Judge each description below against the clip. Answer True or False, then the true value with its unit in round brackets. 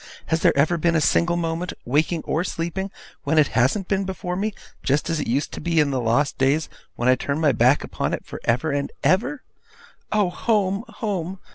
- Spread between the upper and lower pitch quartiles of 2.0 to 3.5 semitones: False (4.8 semitones)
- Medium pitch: True (165 Hz)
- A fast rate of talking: True (215 wpm)